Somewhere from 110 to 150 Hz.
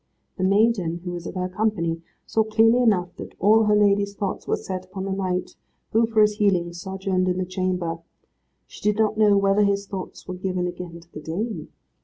No: high, 190 Hz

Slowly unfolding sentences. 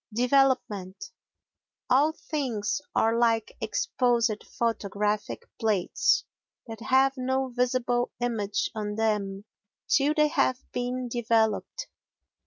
Yes: slow, 95 wpm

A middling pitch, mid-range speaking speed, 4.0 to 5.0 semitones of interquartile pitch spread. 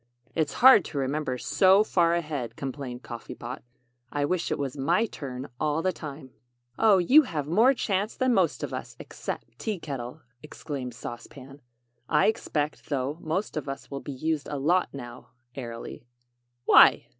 Yes: medium, 150 Hz; average, 165 wpm; average, 4.7 semitones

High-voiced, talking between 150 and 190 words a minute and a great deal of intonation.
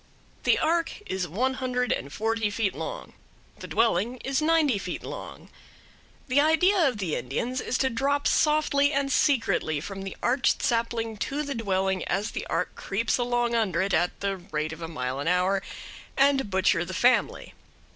Yes: high, 230 Hz; average, 175 wpm; wide, 6.3 semitones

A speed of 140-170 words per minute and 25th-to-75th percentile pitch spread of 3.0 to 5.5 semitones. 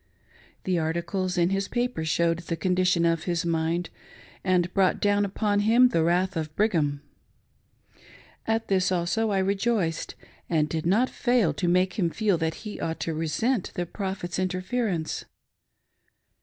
Yes: average, 150 wpm; average, 3.4 semitones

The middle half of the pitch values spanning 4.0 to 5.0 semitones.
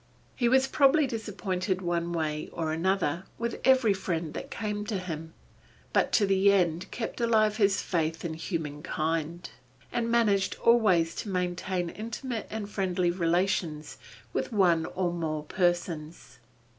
Yes: average, 4.3 semitones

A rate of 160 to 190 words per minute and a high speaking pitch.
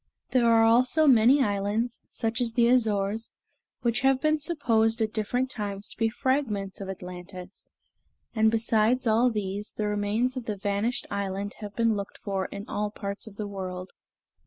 Yes: average, 170 wpm; high, 220 Hz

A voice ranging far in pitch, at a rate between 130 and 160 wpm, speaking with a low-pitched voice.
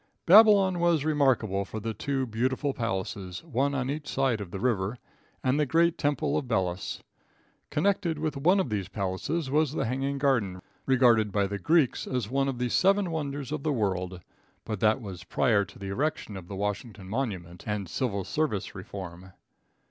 No: wide, 6.6 semitones; average, 180 wpm; low, 125 Hz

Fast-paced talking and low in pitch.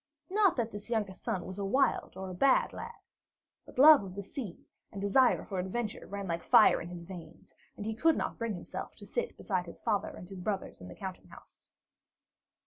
No: fast, 215 wpm; high, 200 Hz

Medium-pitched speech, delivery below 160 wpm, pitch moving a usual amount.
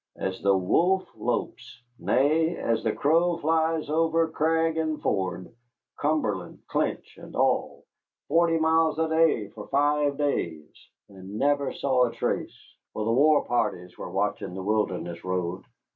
No: medium, 145 Hz; average, 145 wpm; wide, 7.9 semitones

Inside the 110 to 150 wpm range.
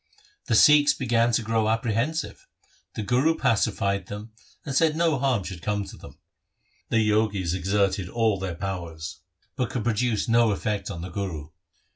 No: average, 160 wpm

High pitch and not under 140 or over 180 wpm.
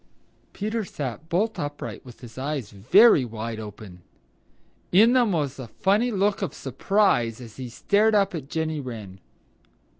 No: medium, 145 Hz; average, 150 wpm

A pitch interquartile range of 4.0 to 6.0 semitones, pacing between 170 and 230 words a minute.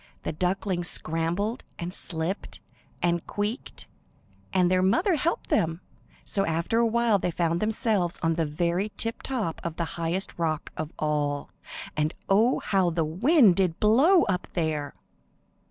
No: average, 4.6 semitones; average, 150 wpm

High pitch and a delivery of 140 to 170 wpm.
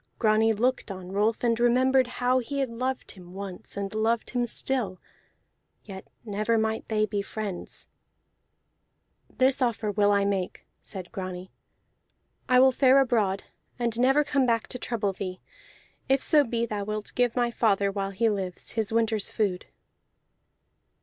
Yes: high, 220 Hz; average, 155 wpm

